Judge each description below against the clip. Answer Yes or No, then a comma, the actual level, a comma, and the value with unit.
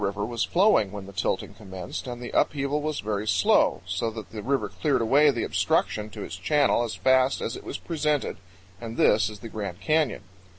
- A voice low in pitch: Yes, low, 115 Hz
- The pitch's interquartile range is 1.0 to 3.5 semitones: No, average, 5.2 semitones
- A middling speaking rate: No, fast, 210 wpm